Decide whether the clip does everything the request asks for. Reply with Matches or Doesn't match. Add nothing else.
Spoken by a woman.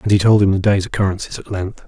Doesn't match